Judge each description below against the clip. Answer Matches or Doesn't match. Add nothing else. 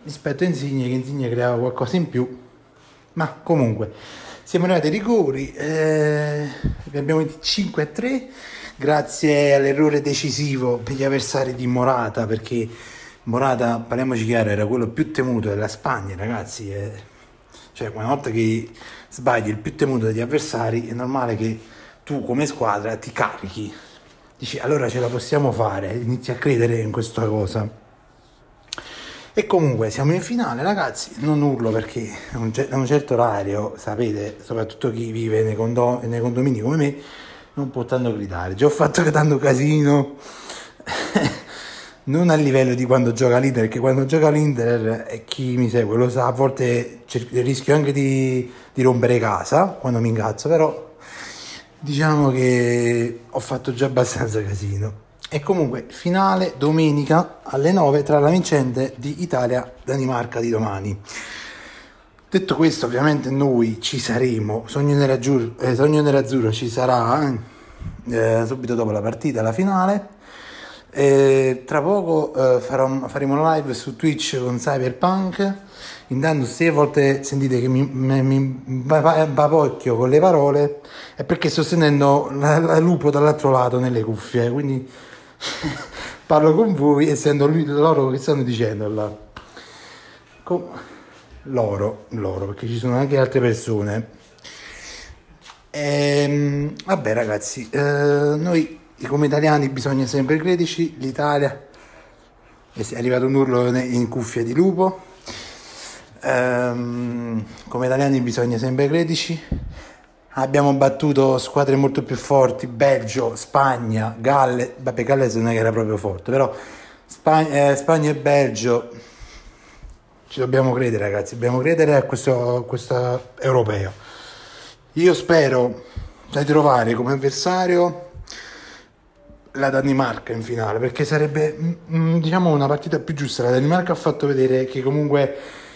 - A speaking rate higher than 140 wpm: Doesn't match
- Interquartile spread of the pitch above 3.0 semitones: Matches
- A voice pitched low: Matches